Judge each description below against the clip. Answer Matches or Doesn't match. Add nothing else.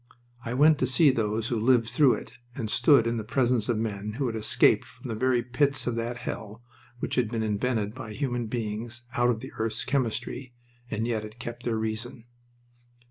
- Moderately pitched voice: Doesn't match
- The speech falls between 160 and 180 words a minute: Doesn't match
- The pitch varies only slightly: Matches